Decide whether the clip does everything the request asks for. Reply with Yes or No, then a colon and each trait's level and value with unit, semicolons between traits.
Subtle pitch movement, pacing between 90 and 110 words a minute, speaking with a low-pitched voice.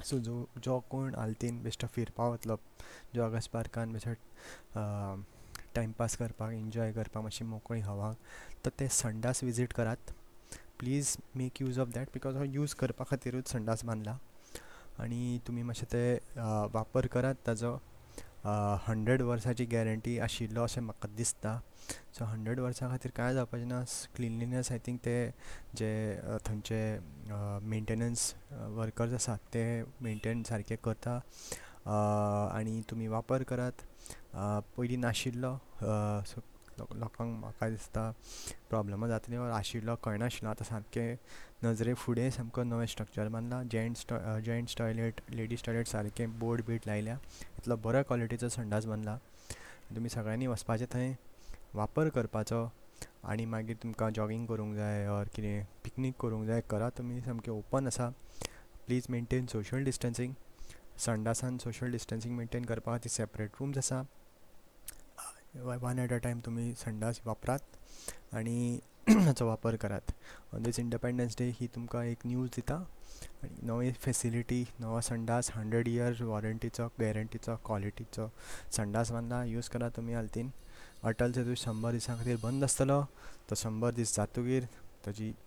No: narrow, 1.9 semitones; average, 125 wpm; low, 115 Hz